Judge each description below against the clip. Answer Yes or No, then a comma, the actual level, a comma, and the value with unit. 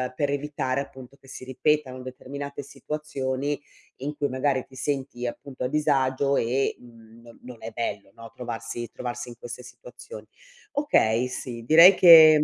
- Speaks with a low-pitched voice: Yes, low, 130 Hz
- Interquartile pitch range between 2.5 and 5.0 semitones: Yes, average, 2.8 semitones